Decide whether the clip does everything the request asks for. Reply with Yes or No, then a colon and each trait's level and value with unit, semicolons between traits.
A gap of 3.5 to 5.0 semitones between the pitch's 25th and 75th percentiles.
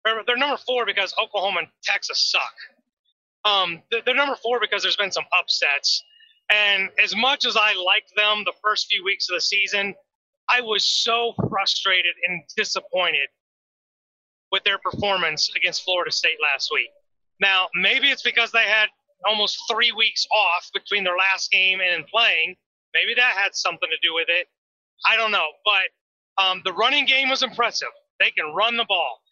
Yes: average, 4.4 semitones